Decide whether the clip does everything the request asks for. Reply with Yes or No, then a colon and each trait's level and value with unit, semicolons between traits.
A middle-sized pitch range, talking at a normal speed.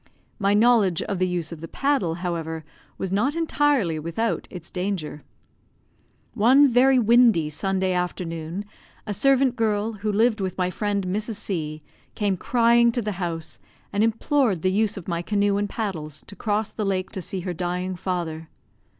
Yes: average, 4.2 semitones; average, 165 wpm